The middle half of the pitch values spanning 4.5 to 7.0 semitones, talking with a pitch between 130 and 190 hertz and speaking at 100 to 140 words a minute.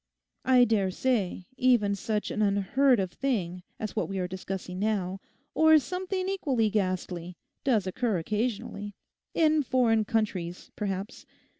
No: average, 5.1 semitones; high, 210 Hz; slow, 135 wpm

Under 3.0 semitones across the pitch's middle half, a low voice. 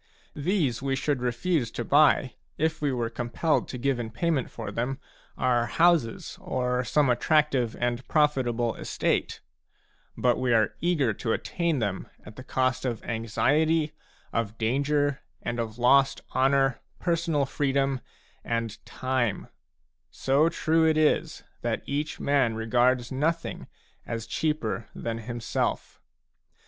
No: average, 4.0 semitones; low, 130 Hz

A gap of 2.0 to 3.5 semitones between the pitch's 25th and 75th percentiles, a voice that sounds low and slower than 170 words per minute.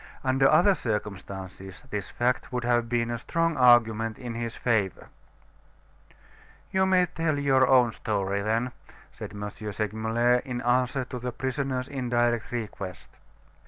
Yes: average, 2.9 semitones; low, 120 Hz; slow, 135 wpm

